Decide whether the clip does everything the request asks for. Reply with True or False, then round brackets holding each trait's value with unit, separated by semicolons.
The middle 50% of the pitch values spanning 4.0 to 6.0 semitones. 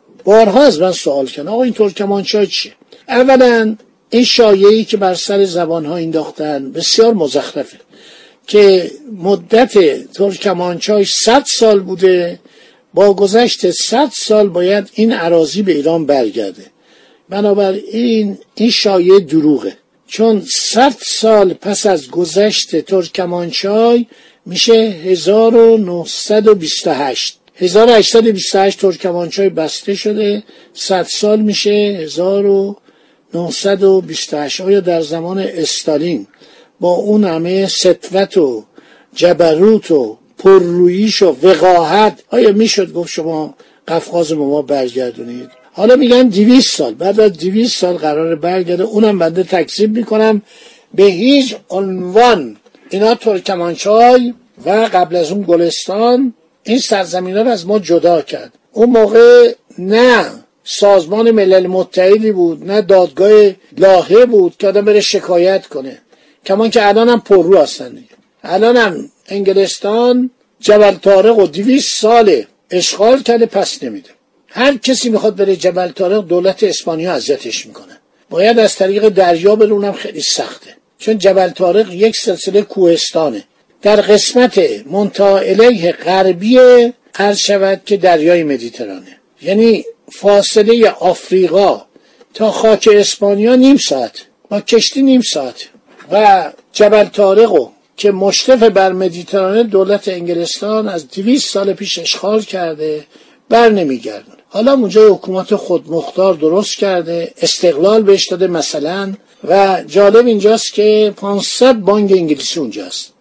False (3.4 semitones)